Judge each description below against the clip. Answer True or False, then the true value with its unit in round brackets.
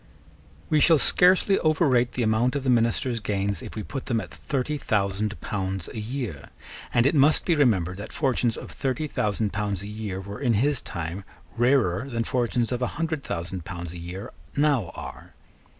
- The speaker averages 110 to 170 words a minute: False (185 wpm)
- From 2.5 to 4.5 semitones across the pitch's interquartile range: False (5.5 semitones)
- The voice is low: True (115 Hz)